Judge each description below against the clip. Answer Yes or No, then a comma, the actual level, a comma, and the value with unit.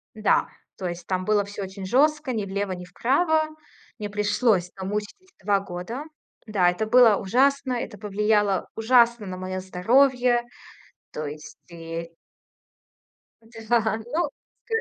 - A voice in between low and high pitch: No, high, 210 Hz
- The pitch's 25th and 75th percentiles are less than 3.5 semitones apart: No, average, 4.7 semitones